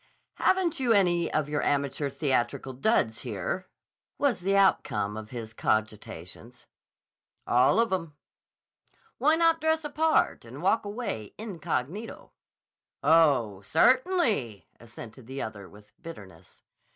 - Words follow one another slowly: Yes, slow, 120 wpm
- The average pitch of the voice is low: No, medium, 145 Hz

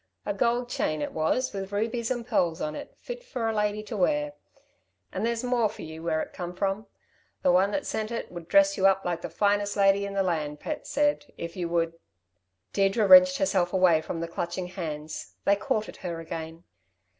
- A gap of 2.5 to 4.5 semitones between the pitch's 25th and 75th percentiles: No, average, 5.2 semitones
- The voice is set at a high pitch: Yes, high, 195 Hz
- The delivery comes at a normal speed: No, fast, 215 wpm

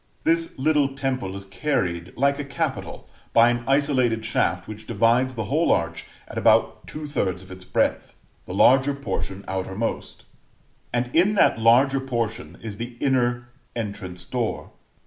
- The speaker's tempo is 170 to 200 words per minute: No, average, 145 wpm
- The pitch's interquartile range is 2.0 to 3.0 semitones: No, average, 5.0 semitones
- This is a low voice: Yes, low, 120 Hz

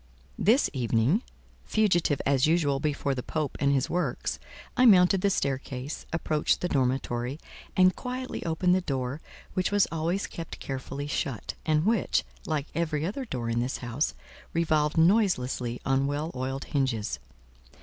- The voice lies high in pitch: No, medium, 150 Hz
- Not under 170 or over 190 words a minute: No, average, 150 wpm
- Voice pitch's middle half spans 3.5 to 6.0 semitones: Yes, average, 5.0 semitones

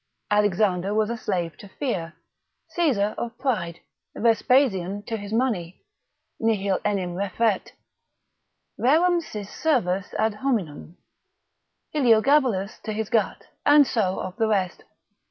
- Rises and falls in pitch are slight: No, average, 4.3 semitones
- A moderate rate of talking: No, slow, 120 wpm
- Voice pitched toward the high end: Yes, high, 210 Hz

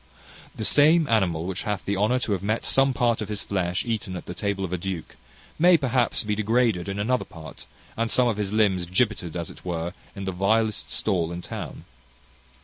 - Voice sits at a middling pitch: No, low, 100 Hz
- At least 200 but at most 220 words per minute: Yes, fast, 205 wpm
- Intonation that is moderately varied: Yes, average, 4.0 semitones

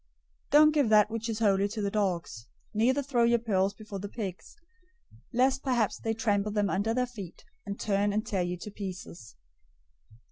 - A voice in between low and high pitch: No, high, 210 Hz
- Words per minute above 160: Yes, average, 185 wpm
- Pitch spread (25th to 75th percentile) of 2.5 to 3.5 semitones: Yes, average, 2.9 semitones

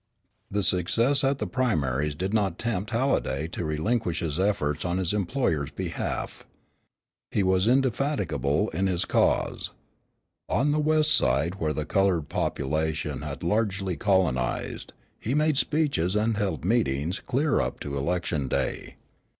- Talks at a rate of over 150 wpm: No, average, 140 wpm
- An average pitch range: No, wide, 7.1 semitones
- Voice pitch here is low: Yes, very low, 95 Hz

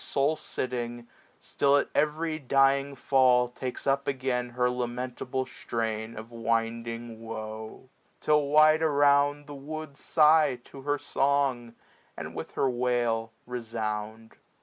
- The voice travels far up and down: No, average, 3.4 semitones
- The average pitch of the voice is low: Yes, low, 125 Hz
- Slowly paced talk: Yes, slow, 125 wpm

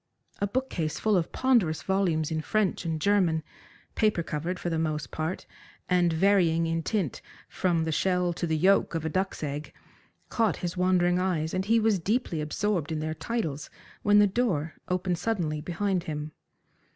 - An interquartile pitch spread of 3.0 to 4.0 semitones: Yes, average, 3.7 semitones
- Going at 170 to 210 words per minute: Yes, average, 175 wpm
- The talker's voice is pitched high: No, medium, 175 Hz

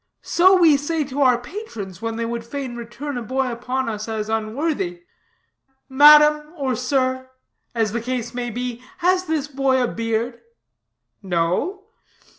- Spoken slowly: No, average, 150 wpm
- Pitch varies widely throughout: No, average, 4.4 semitones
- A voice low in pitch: No, very high, 255 Hz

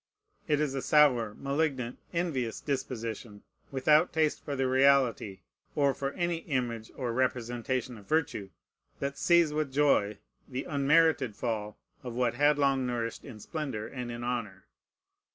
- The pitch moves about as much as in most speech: Yes, average, 3.8 semitones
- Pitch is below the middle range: Yes, low, 130 Hz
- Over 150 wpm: No, average, 145 wpm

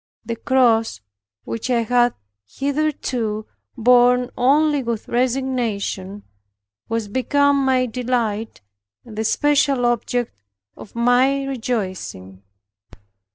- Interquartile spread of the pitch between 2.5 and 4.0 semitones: Yes, average, 2.8 semitones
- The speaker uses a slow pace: Yes, slow, 95 wpm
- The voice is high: Yes, high, 245 Hz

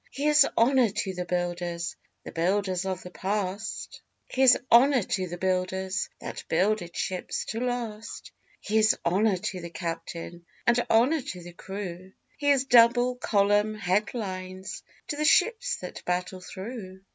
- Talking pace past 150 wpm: No, average, 145 wpm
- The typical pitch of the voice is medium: No, high, 195 Hz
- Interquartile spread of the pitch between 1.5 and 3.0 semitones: No, average, 4.6 semitones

